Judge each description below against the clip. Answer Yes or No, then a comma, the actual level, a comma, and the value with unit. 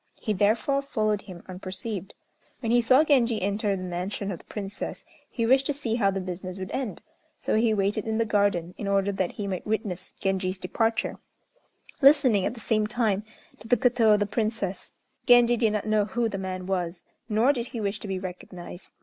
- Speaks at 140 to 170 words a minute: No, average, 200 wpm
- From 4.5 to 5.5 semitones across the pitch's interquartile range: No, average, 3.2 semitones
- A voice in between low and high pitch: No, high, 210 Hz